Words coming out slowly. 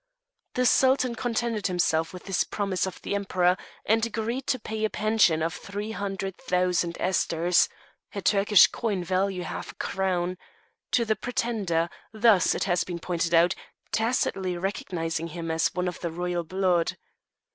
Yes: slow, 130 wpm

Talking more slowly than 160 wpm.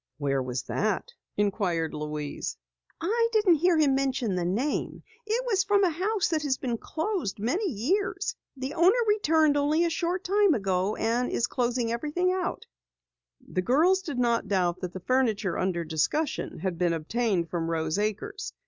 No: average, 165 wpm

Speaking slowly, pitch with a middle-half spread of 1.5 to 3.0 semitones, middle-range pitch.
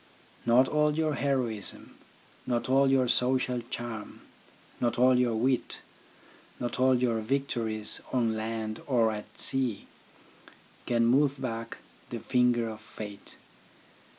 No: slow, 125 wpm; narrow, 2.6 semitones; low, 120 Hz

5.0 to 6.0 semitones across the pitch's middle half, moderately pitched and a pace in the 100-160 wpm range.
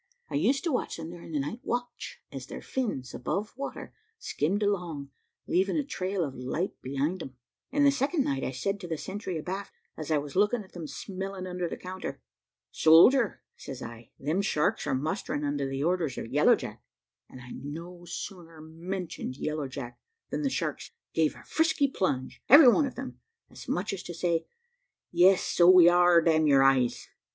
No: average, 5.3 semitones; medium, 175 Hz; average, 190 wpm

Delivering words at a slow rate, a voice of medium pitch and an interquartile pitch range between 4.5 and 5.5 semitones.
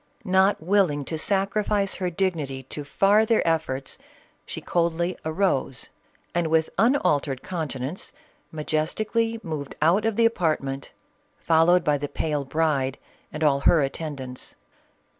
Yes: slow, 125 wpm; medium, 160 Hz; average, 4.8 semitones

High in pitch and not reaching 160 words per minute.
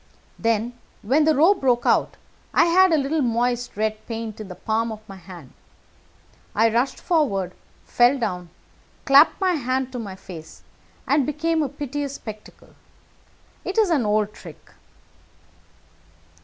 Yes: high, 240 Hz; average, 145 wpm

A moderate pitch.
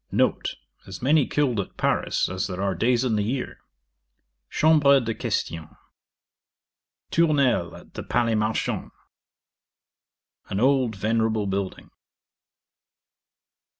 No: low, 115 Hz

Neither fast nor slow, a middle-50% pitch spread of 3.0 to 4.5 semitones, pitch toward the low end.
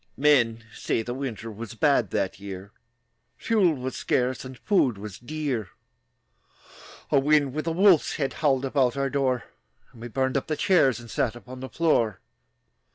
Yes: average, 165 wpm; average, 4.1 semitones; low, 130 Hz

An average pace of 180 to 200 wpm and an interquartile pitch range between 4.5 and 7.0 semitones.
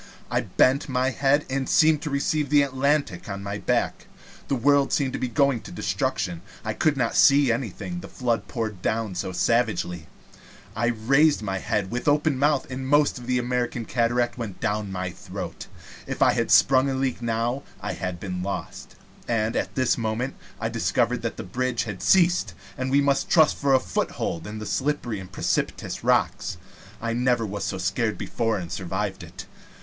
Yes: average, 185 wpm; average, 4.8 semitones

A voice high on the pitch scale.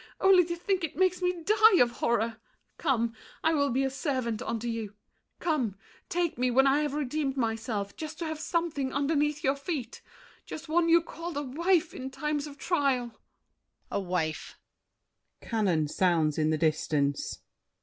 Yes: very high, 275 Hz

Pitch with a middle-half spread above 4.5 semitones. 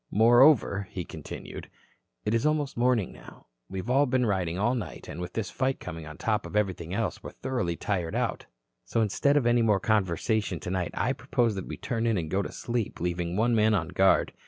Yes: average, 4.9 semitones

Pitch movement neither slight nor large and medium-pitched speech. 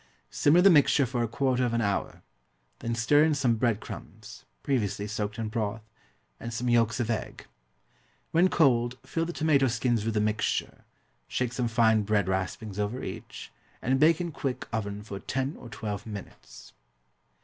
No: average, 3.8 semitones; low, 115 Hz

